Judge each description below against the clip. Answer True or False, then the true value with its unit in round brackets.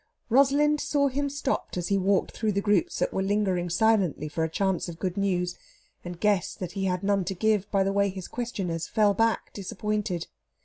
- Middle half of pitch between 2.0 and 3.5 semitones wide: True (3.1 semitones)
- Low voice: False (200 Hz)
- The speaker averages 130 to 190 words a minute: False (205 wpm)